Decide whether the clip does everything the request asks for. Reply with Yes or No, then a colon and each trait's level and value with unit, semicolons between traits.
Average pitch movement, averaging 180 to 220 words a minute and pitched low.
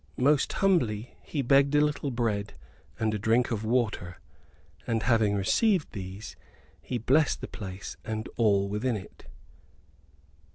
No: average, 4.7 semitones; slow, 135 wpm; low, 115 Hz